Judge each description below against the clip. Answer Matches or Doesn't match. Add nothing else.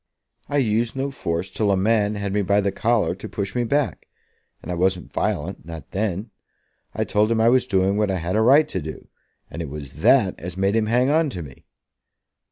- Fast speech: Matches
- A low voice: Matches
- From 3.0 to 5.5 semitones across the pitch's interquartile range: Matches